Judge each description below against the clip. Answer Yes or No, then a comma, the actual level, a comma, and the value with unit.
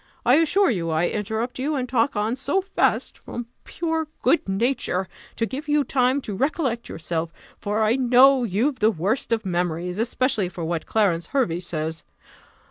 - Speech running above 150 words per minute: Yes, average, 170 wpm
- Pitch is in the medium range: No, high, 230 Hz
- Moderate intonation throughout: No, wide, 6.8 semitones